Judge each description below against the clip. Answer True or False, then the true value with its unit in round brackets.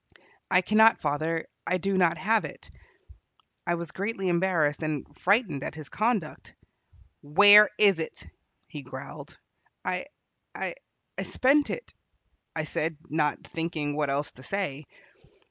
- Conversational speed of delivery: False (130 wpm)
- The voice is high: False (170 Hz)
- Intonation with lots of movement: False (4.9 semitones)